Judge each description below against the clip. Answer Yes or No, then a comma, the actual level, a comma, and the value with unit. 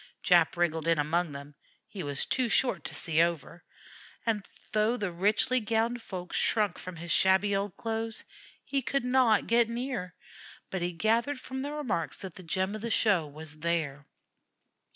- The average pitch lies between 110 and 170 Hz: No, high, 195 Hz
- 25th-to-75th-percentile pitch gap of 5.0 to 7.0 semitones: Yes, wide, 5.4 semitones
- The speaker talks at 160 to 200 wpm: Yes, average, 175 wpm